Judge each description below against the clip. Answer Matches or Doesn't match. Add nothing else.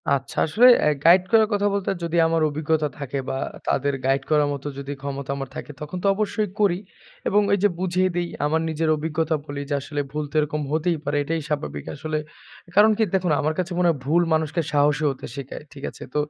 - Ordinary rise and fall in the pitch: Matches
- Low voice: Doesn't match